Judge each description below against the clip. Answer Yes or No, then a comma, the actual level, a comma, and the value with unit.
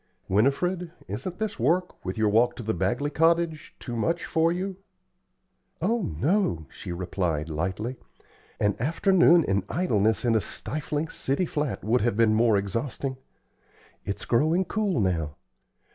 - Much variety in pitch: Yes, wide, 8.5 semitones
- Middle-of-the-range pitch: No, low, 125 Hz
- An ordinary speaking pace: Yes, average, 145 wpm